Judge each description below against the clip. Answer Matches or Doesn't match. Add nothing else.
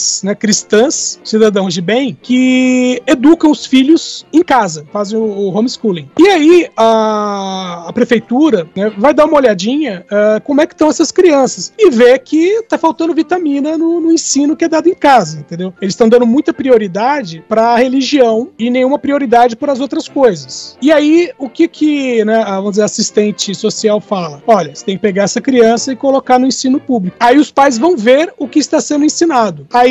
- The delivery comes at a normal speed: Doesn't match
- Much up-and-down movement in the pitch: Matches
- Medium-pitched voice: Doesn't match